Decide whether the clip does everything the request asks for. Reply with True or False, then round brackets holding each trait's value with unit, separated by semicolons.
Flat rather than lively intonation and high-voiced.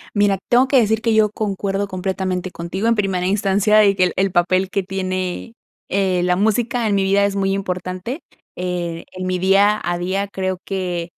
True (1.9 semitones; 195 Hz)